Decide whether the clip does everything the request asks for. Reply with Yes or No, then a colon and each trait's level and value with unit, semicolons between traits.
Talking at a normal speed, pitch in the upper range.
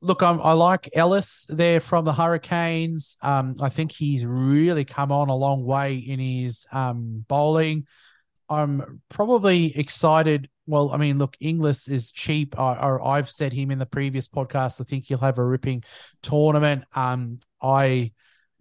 No: average, 160 wpm; medium, 140 Hz